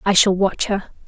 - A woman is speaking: Yes, female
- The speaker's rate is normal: No, fast, 225 wpm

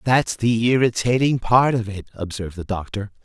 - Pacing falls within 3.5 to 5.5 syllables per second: Yes, 5.1 syllables/s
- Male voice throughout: Yes, male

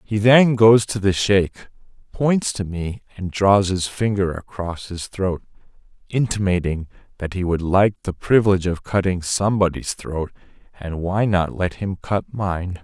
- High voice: No, very low, 95 Hz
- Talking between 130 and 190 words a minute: Yes, average, 160 wpm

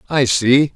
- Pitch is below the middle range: Yes, low, 130 Hz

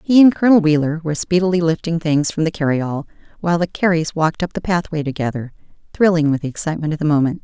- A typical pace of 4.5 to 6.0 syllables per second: No, 6.9 syllables/s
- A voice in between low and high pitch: Yes, medium, 165 Hz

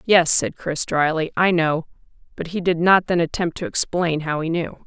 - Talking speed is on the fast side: Yes, fast, 210 wpm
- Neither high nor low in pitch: Yes, medium, 165 Hz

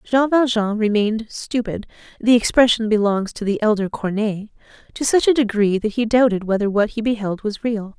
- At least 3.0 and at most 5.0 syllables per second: No, 5.5 syllables/s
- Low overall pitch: No, high, 220 Hz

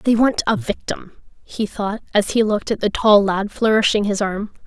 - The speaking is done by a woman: Yes, female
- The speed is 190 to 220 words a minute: Yes, fast, 205 wpm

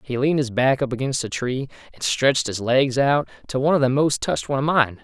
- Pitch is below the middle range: Yes, low, 130 Hz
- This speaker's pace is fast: Yes, fast, 260 wpm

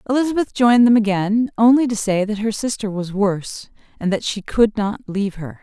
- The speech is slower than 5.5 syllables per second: No, 5.6 syllables/s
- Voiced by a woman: Yes, female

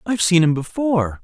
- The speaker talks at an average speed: No, fast, 245 wpm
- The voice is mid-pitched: Yes, medium, 180 Hz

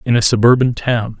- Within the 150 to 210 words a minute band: Yes, average, 200 wpm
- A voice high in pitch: No, low, 115 Hz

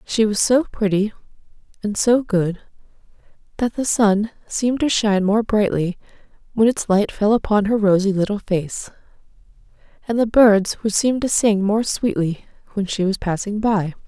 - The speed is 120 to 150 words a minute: No, average, 160 wpm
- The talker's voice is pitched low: No, high, 210 Hz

